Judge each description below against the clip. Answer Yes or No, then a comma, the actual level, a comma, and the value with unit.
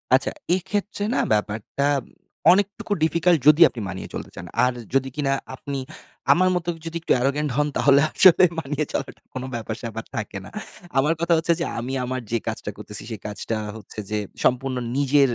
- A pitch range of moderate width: No, wide, 5.8 semitones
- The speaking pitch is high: No, medium, 140 Hz